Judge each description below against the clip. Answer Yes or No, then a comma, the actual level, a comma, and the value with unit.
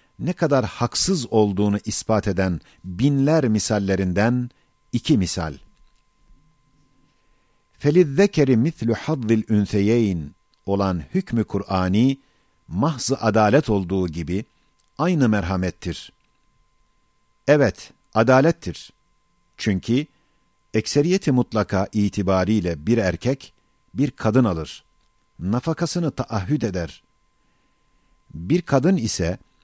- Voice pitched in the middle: No, low, 115 Hz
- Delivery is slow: Yes, slow, 80 wpm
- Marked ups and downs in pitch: Yes, wide, 6.5 semitones